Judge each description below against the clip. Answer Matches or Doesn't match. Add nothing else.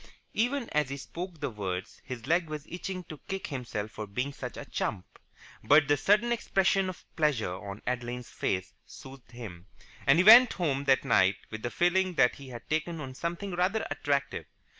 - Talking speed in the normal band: Matches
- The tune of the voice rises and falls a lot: Matches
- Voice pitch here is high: Doesn't match